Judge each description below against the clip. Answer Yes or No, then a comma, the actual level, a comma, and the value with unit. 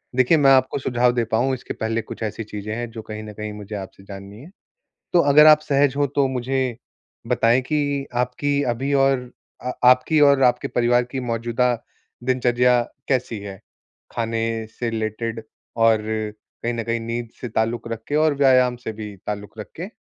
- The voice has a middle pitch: No, low, 120 Hz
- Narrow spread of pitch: No, average, 3.0 semitones